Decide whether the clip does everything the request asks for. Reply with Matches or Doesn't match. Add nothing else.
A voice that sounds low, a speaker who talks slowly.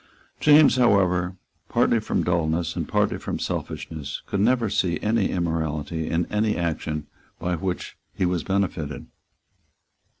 Matches